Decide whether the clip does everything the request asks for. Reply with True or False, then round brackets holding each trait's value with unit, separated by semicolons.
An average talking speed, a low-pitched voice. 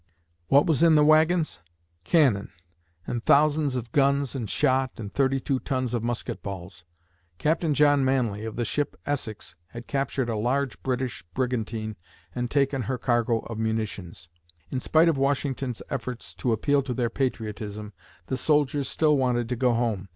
True (165 wpm; 125 Hz)